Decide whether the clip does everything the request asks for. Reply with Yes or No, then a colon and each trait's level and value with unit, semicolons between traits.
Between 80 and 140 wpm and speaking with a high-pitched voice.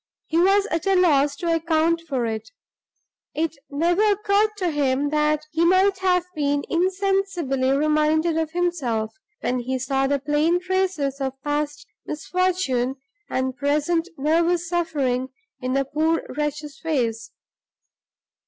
Yes: slow, 135 wpm; very high, 305 Hz